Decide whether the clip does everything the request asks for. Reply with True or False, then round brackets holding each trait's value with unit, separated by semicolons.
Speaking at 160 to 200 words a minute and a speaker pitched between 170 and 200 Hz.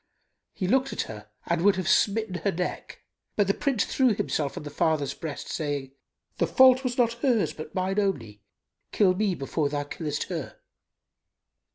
True (175 wpm; 185 Hz)